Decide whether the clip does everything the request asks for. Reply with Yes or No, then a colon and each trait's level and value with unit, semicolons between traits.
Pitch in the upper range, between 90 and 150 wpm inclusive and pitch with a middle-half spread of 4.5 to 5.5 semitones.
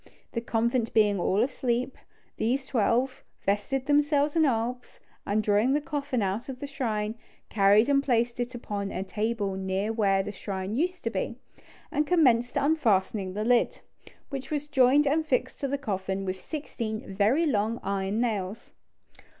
No: high, 235 Hz; average, 160 wpm; average, 5.1 semitones